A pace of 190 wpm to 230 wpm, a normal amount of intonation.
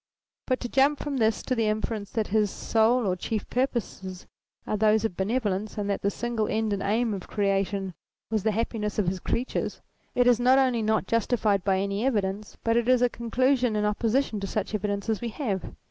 Yes: average, 200 wpm; average, 3.0 semitones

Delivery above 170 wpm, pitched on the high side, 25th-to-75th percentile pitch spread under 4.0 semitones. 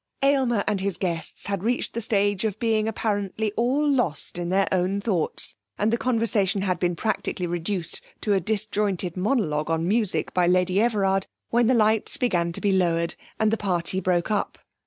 Yes: average, 180 wpm; high, 200 Hz; average, 3.5 semitones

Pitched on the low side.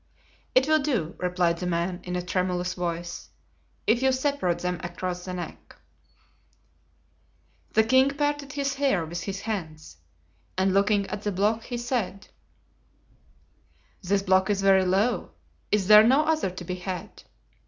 No: high, 195 Hz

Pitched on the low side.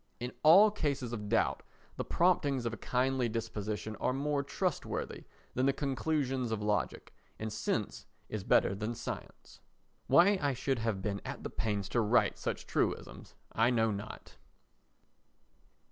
Yes: low, 120 Hz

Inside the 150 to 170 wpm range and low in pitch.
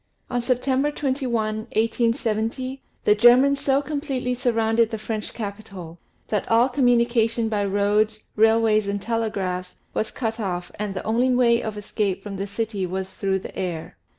No: average, 160 wpm; high, 225 Hz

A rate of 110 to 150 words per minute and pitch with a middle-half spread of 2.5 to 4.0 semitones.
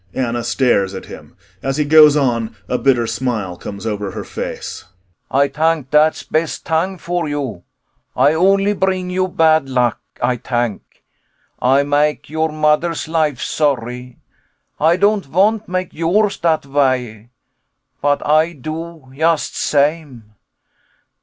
No: slow, 135 wpm; average, 4.7 semitones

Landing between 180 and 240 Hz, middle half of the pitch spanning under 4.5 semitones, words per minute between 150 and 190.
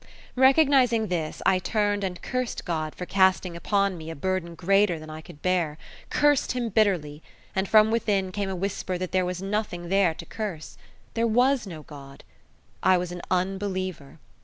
Yes: medium, 185 Hz; average, 3.4 semitones; average, 175 wpm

